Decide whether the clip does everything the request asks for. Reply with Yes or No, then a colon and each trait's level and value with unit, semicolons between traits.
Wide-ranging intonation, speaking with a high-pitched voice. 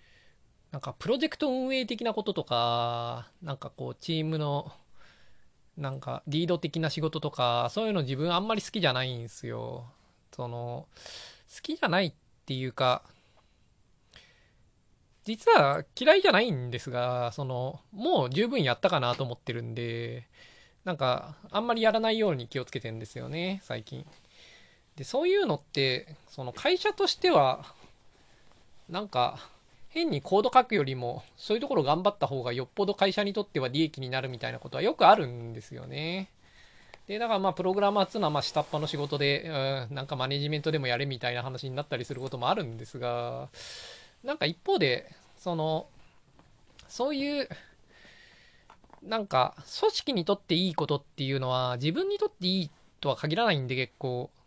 No: wide, 8.0 semitones; medium, 150 Hz